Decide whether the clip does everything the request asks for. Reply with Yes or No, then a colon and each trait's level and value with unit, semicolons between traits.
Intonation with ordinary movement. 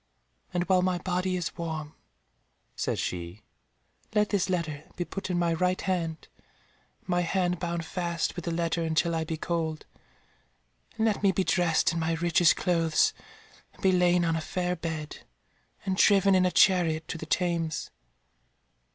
No: narrow, 1.9 semitones